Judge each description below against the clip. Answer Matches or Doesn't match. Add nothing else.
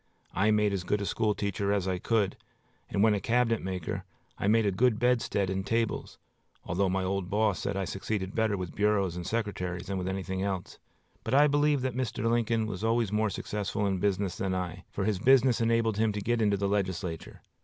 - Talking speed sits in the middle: Doesn't match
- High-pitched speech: Doesn't match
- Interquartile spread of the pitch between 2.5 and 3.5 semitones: Matches